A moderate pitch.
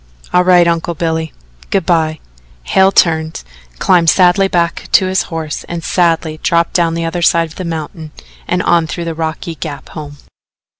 Yes: medium, 165 Hz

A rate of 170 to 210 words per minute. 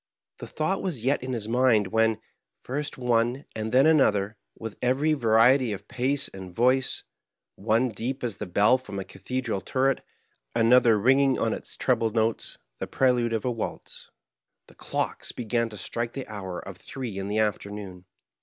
Yes: average, 175 wpm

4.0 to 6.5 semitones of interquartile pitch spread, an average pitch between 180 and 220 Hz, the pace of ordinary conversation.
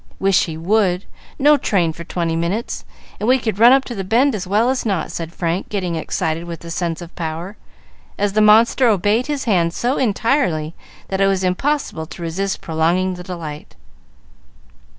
Yes: average, 4.8 semitones; high, 190 Hz; average, 185 wpm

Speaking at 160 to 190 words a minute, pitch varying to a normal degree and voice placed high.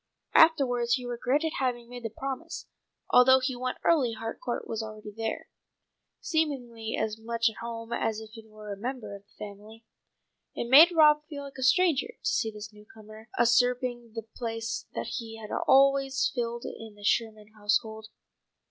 Yes: average, 165 wpm; average, 3.1 semitones; high, 235 Hz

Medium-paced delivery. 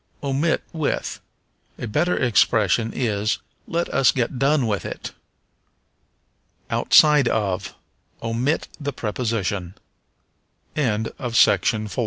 No: slow, 95 wpm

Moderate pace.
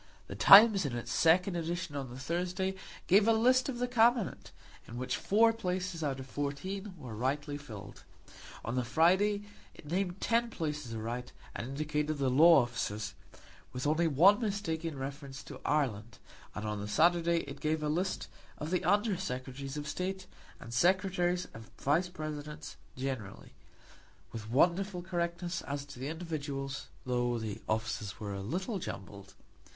Yes: average, 160 wpm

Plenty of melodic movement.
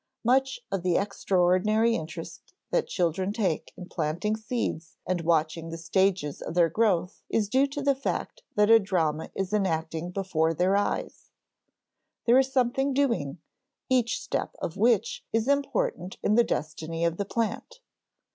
Yes: wide, 5.8 semitones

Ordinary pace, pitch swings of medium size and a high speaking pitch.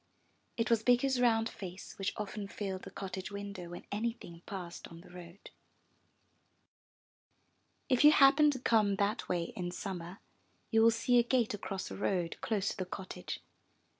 Yes: average, 165 wpm; average, 3.9 semitones; high, 200 Hz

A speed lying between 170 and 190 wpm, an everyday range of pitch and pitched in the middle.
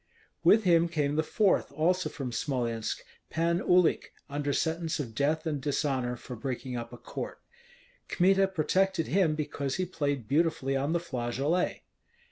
No: average, 150 wpm; average, 4.3 semitones; medium, 150 Hz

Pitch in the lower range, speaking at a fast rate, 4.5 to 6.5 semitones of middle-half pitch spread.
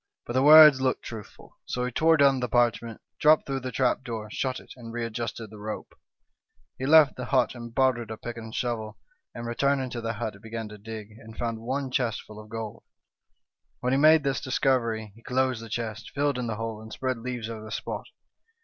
No: low, 120 Hz; fast, 215 wpm; average, 2.7 semitones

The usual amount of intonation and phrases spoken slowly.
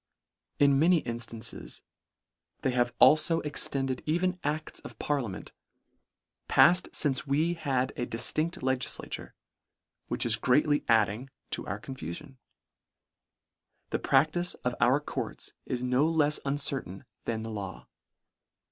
Yes: average, 4.0 semitones; slow, 125 wpm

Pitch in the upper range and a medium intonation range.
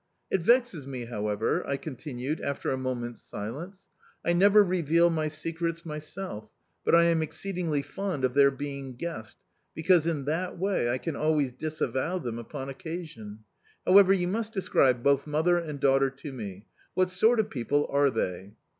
No: medium, 150 Hz; average, 5.0 semitones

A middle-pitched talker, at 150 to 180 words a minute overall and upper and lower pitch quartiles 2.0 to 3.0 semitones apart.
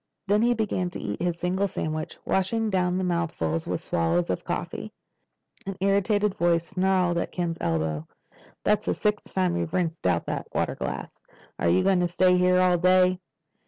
Yes: medium, 180 Hz; average, 175 wpm; narrow, 2.5 semitones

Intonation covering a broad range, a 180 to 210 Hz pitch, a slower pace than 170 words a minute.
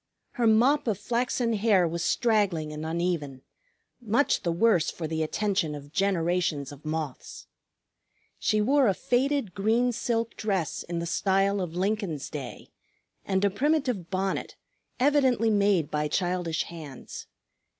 Yes: wide, 5.7 semitones; high, 190 Hz; average, 140 wpm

